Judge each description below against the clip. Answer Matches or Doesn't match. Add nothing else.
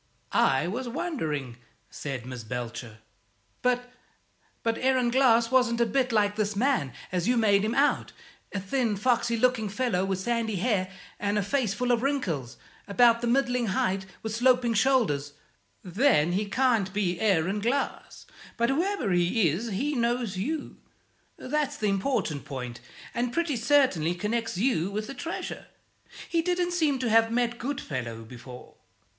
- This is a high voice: Matches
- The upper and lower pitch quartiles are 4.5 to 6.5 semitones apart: Matches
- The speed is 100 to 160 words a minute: Matches